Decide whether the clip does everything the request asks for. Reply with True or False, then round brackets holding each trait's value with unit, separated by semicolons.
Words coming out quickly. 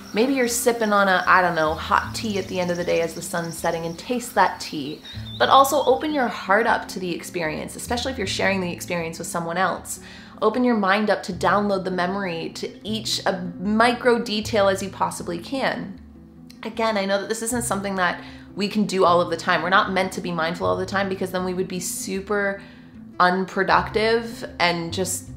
True (220 wpm)